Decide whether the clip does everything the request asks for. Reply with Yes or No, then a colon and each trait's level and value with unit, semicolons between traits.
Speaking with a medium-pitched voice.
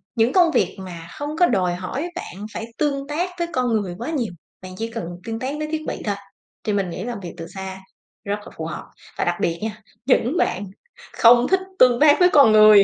No: high, 225 Hz